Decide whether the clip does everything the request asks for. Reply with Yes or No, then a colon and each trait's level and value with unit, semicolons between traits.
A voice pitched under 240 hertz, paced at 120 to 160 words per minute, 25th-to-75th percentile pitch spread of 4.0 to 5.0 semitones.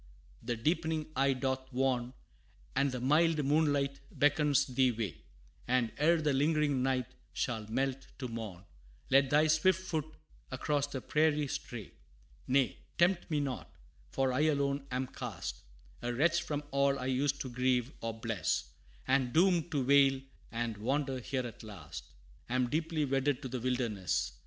No: low, 135 Hz; average, 155 wpm; average, 3.1 semitones